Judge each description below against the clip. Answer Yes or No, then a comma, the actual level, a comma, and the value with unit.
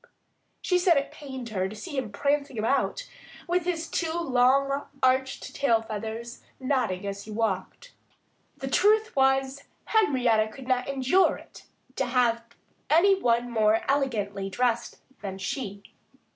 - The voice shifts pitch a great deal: No, average, 4.2 semitones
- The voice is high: Yes, very high, 255 Hz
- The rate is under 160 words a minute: Yes, average, 140 wpm